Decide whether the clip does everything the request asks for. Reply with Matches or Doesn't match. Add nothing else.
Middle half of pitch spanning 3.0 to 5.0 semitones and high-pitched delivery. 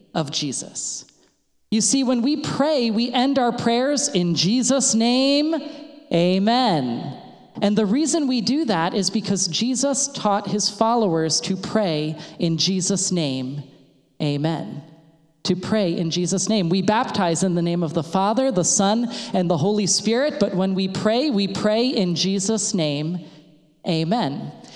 Doesn't match